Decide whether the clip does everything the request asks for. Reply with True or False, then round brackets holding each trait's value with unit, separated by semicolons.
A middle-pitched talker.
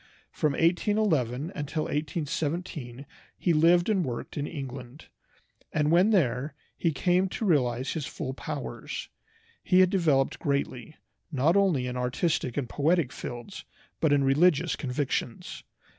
True (150 Hz)